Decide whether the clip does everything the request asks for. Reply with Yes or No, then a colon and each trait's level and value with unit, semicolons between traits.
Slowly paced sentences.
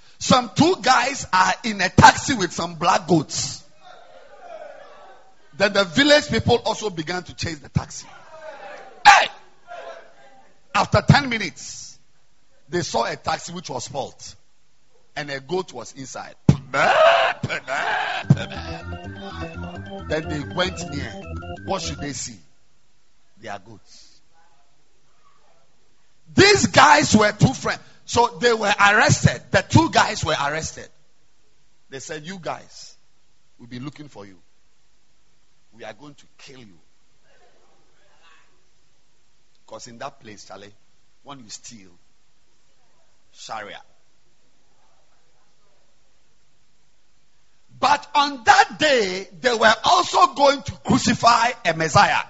Yes: slow, 110 wpm